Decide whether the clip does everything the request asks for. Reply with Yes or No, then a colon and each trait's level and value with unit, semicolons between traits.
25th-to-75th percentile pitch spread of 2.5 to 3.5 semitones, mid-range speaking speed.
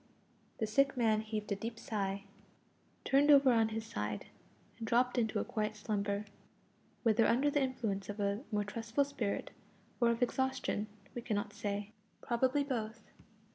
Yes: average, 3.2 semitones; average, 155 wpm